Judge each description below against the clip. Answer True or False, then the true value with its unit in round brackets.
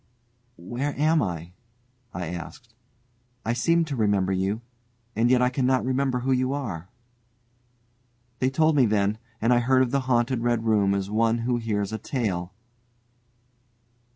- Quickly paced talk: False (155 wpm)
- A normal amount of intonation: True (4.1 semitones)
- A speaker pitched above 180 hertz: False (120 Hz)